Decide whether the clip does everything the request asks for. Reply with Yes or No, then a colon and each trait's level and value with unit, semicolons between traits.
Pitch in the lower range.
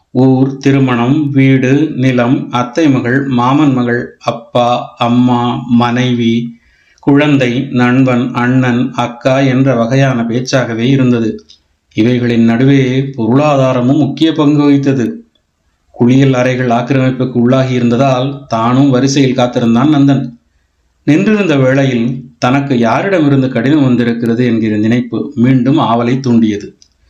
Yes: low, 125 Hz